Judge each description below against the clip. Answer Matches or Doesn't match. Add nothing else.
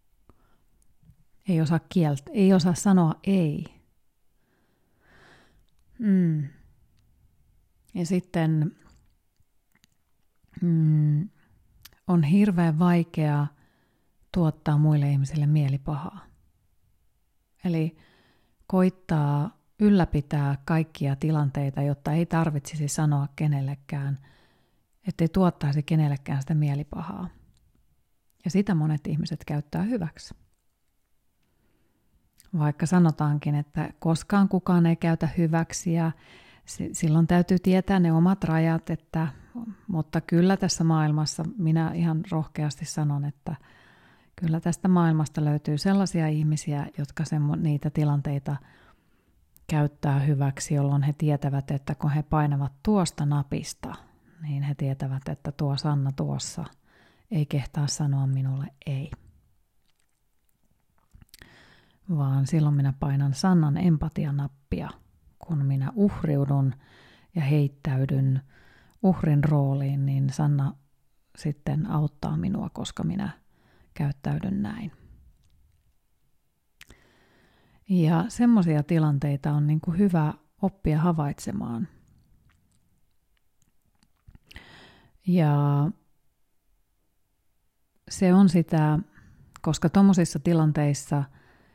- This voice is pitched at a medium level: Matches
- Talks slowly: Matches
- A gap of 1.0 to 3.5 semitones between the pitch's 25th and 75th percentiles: Matches